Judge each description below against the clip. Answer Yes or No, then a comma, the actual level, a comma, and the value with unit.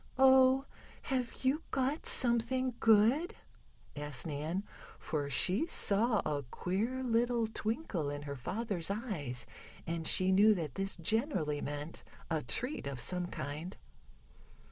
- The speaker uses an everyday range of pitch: No, wide, 8.4 semitones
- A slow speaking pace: Yes, slow, 125 wpm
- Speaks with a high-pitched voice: Yes, high, 200 Hz